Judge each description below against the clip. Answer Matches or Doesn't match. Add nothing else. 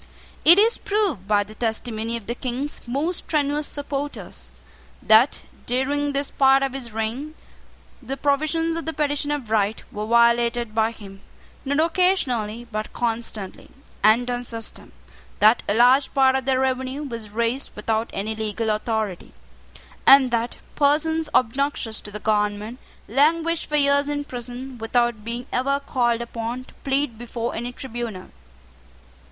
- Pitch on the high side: Matches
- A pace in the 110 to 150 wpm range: Matches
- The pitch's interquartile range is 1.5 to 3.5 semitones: Doesn't match